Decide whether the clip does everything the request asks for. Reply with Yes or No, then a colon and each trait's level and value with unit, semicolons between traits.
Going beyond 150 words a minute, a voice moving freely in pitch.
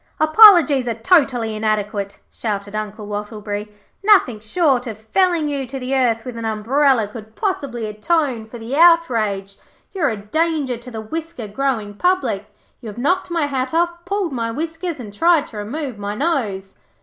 Yes: average, 170 wpm; wide, 6.8 semitones